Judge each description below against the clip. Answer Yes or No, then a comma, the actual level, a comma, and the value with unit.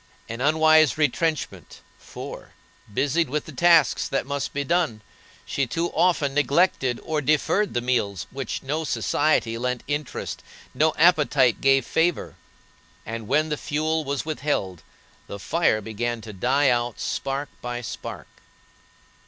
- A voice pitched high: No, medium, 140 Hz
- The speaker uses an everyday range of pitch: Yes, average, 4.4 semitones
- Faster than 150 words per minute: No, average, 140 wpm